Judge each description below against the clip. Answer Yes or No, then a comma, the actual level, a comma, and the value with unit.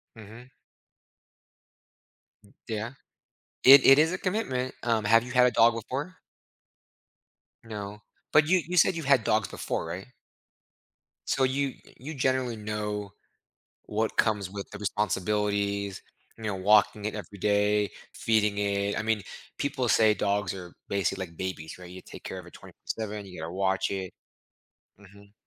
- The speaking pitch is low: Yes, low, 105 Hz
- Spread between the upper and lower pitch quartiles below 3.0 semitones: No, average, 3.5 semitones